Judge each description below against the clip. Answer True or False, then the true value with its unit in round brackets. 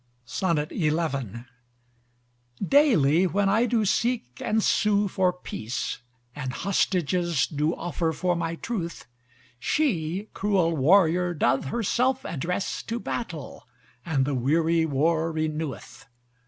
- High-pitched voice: False (170 Hz)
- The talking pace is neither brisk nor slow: False (110 wpm)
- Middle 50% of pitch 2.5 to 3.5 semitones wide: False (4.7 semitones)